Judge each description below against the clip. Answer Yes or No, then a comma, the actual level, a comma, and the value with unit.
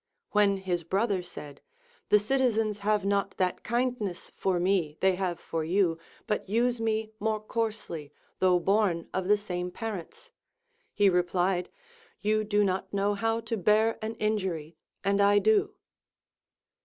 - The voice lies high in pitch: Yes, high, 200 Hz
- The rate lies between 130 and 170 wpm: Yes, average, 150 wpm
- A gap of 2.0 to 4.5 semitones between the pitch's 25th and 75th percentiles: Yes, average, 3.2 semitones